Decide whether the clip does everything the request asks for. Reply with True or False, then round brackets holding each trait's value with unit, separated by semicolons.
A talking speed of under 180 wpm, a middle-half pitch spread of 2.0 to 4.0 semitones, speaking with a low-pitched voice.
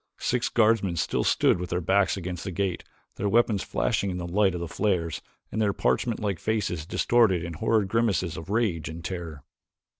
False (190 wpm; 3.7 semitones; 95 Hz)